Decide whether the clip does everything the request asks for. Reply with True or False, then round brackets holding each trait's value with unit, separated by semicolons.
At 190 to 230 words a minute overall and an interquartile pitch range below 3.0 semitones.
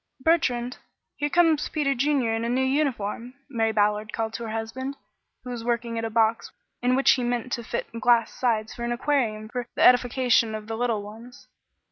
True (195 wpm; 2.6 semitones)